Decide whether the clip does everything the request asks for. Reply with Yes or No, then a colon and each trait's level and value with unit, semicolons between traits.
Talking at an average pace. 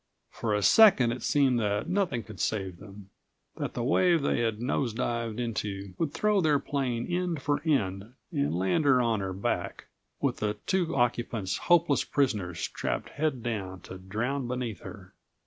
Yes: average, 170 wpm